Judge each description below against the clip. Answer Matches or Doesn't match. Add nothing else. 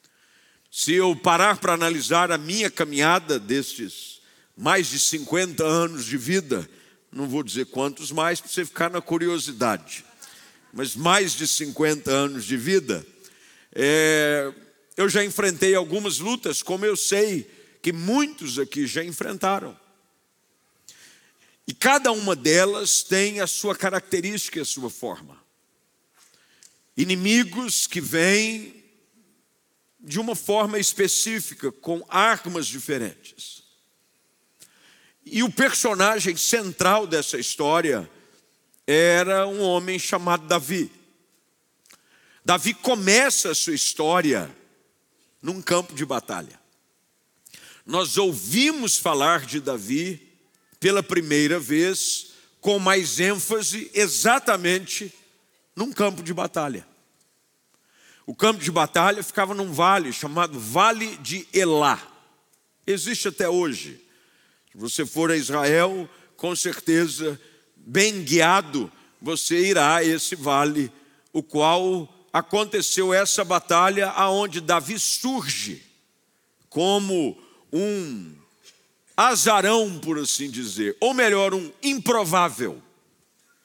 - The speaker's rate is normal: Doesn't match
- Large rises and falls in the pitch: Doesn't match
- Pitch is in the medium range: Matches